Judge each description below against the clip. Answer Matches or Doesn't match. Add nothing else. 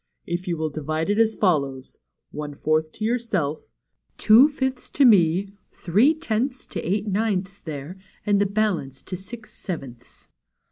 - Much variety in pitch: Matches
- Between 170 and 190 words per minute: Doesn't match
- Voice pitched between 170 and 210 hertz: Matches